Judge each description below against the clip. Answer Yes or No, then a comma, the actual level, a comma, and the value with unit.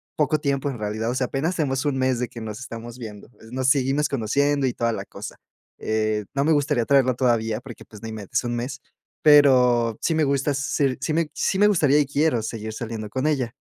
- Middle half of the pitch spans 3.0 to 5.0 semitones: Yes, average, 3.7 semitones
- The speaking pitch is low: Yes, low, 130 Hz